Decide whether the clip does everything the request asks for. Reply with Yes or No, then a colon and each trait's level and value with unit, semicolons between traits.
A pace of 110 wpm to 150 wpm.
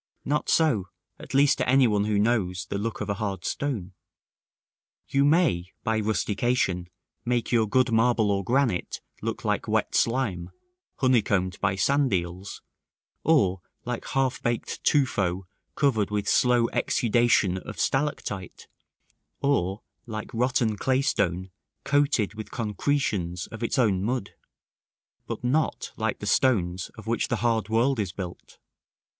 Yes: average, 140 wpm